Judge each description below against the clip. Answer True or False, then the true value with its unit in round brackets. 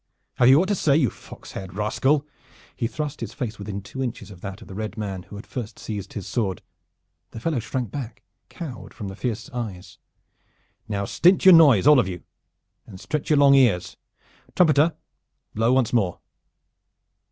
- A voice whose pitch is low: True (115 Hz)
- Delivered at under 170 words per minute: False (185 wpm)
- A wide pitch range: True (5.7 semitones)